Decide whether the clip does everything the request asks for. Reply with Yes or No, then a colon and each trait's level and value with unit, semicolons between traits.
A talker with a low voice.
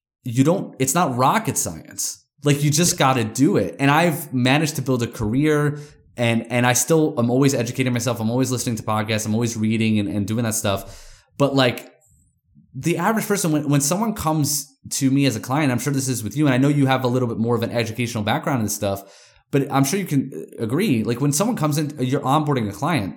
Yes: low, 130 Hz